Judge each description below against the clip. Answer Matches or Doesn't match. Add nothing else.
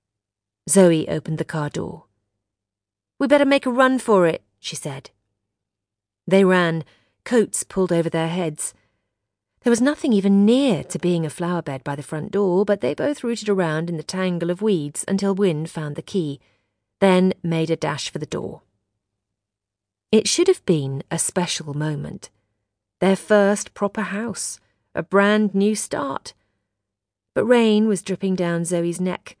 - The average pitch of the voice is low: Doesn't match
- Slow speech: Doesn't match